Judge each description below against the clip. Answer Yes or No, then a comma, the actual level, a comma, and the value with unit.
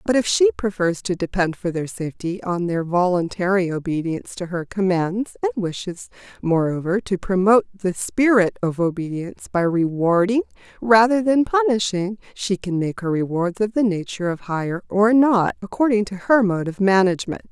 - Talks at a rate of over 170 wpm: No, average, 165 wpm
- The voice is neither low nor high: No, high, 195 Hz